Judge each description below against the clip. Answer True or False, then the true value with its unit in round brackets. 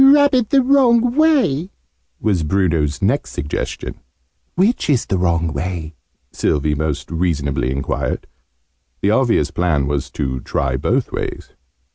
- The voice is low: True (90 Hz)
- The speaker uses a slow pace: True (130 wpm)